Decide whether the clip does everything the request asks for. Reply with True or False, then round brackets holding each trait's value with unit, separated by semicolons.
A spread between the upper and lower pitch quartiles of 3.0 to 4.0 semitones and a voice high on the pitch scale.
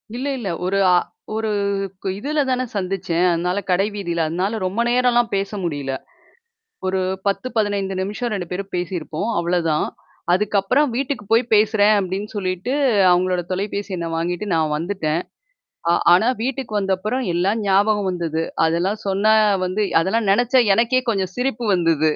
True (3.6 semitones; 195 Hz)